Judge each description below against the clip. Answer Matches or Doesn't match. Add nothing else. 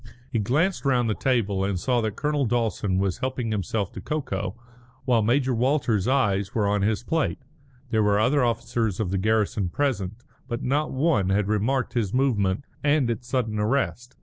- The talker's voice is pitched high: Doesn't match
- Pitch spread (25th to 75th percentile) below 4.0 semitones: Doesn't match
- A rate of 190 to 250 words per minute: Doesn't match